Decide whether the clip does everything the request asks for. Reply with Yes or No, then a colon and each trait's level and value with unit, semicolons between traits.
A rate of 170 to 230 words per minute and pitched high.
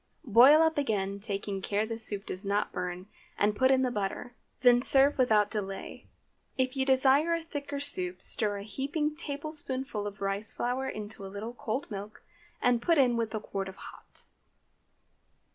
Yes: average, 175 wpm; high, 230 Hz